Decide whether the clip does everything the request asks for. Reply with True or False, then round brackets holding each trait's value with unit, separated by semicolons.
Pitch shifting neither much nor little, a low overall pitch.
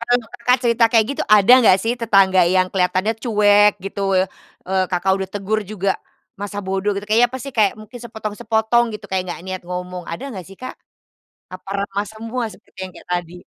False (3.3 semitones; 205 Hz)